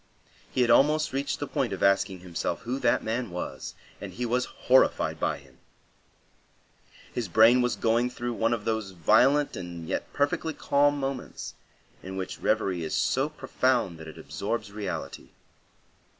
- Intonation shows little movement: No, average, 5.3 semitones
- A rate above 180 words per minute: No, average, 160 wpm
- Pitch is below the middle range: Yes, low, 115 Hz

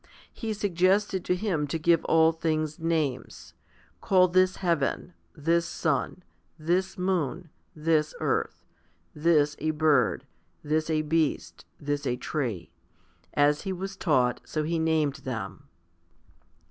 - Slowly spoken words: Yes, slow, 125 wpm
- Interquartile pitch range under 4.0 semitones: Yes, average, 3.2 semitones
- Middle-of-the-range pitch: Yes, medium, 160 Hz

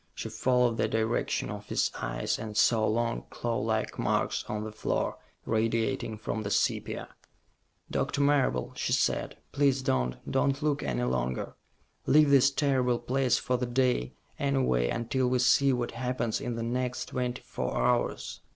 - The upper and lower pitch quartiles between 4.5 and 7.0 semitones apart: No, average, 3.1 semitones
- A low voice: Yes, low, 120 Hz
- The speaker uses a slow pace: No, average, 155 wpm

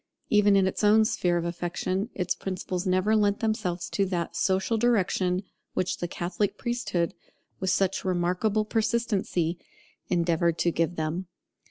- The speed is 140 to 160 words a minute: Yes, average, 150 wpm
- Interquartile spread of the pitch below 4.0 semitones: Yes, average, 3.0 semitones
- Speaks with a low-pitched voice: No, medium, 185 Hz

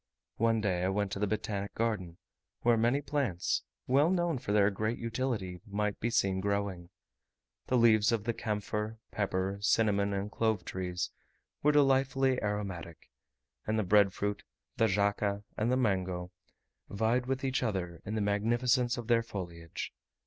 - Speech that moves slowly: No, average, 155 wpm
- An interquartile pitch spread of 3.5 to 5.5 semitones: No, average, 3.1 semitones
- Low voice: Yes, low, 105 Hz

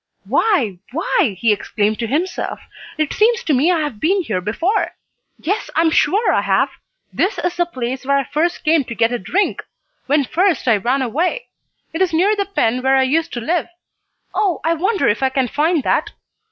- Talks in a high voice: Yes, very high, 310 Hz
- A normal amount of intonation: No, wide, 6.3 semitones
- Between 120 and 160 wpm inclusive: No, fast, 205 wpm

